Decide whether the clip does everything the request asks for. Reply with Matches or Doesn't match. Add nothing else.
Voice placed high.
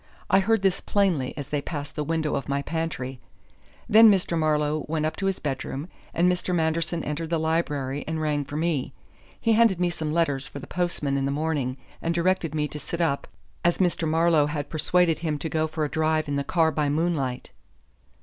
Doesn't match